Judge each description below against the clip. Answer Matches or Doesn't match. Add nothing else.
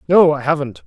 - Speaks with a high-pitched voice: Doesn't match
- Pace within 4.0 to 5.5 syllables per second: Doesn't match